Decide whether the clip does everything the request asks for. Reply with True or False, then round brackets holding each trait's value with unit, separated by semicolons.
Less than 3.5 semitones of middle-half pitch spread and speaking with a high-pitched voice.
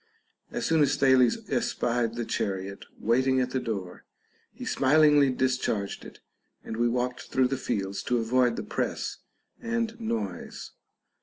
False (2.9 semitones; 125 Hz)